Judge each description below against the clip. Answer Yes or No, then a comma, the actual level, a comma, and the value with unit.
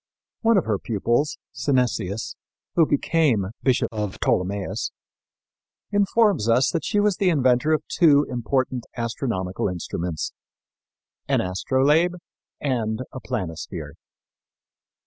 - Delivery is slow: Yes, slow, 110 wpm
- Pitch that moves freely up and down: Yes, wide, 6.8 semitones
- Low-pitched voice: Yes, low, 125 Hz